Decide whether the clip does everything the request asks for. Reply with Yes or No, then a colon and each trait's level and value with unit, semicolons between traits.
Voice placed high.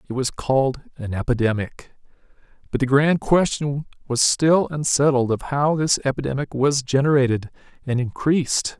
No: low, 135 Hz